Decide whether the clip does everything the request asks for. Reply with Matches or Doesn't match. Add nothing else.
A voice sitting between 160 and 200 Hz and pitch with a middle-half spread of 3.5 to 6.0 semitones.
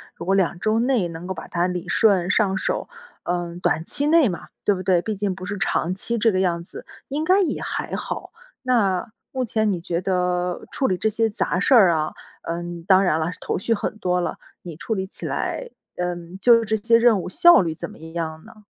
Matches